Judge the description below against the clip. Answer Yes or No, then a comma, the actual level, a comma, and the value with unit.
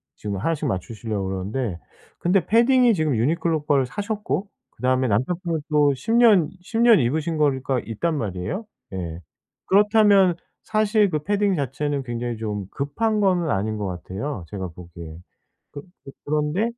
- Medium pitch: Yes, medium, 145 Hz